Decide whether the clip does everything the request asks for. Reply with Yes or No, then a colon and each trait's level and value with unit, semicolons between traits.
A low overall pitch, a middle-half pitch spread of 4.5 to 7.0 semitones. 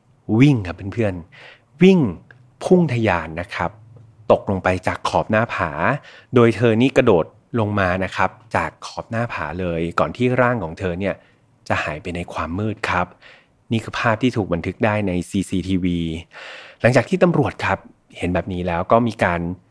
Yes: low, 100 Hz; average, 5.0 semitones